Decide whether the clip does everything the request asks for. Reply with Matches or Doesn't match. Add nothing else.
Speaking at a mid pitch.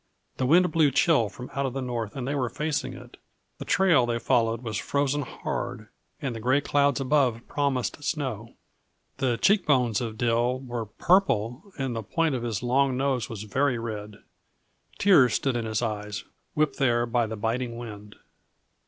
Doesn't match